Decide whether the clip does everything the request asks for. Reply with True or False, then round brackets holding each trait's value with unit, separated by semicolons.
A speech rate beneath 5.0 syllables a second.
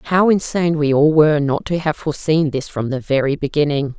False (5.6 syllables/s)